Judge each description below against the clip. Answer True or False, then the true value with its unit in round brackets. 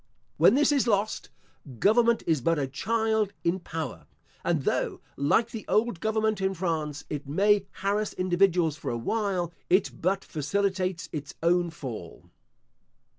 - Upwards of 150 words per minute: False (145 wpm)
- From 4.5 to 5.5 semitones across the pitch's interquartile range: True (4.8 semitones)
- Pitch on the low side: False (185 Hz)